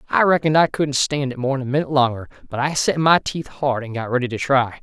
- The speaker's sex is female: No, male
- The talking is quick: Yes, fast, 260 wpm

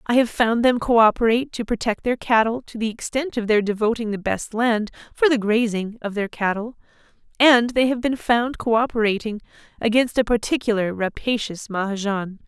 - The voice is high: Yes, high, 225 Hz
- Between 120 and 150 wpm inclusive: No, average, 175 wpm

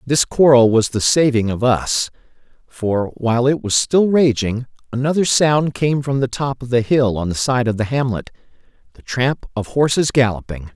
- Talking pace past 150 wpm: Yes, average, 180 wpm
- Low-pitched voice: Yes, low, 125 Hz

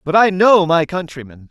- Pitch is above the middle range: No, medium, 170 Hz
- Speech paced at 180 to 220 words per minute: Yes, average, 200 wpm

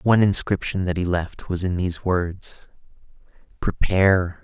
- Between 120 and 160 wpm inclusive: Yes, slow, 135 wpm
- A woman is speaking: No, male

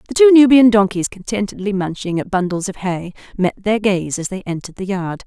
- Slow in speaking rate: No, fast, 205 wpm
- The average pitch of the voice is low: No, high, 200 Hz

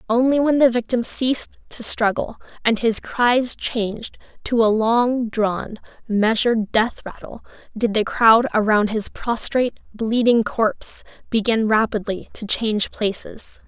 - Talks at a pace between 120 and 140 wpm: Yes, slow, 135 wpm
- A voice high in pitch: Yes, high, 225 Hz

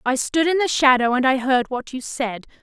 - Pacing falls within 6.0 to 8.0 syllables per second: No, 5.0 syllables/s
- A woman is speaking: Yes, female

